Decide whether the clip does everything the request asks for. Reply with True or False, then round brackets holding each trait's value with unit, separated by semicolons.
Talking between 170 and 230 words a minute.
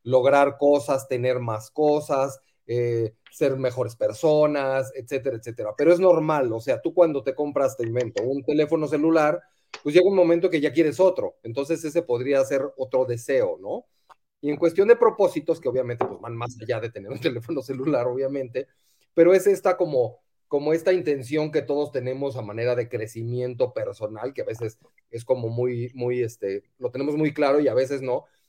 True (185 wpm)